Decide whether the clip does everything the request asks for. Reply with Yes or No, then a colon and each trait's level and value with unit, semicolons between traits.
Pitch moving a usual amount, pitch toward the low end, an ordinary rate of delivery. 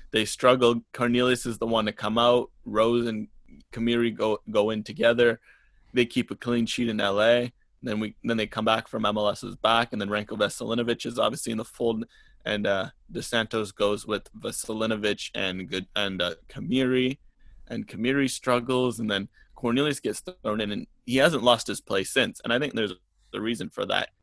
No: narrow, 2.2 semitones; low, 115 Hz; average, 190 wpm